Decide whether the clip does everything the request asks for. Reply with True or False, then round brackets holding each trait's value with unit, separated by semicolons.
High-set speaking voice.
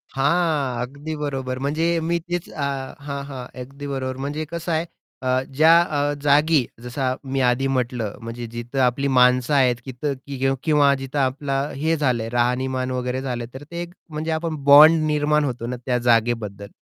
False (135 Hz)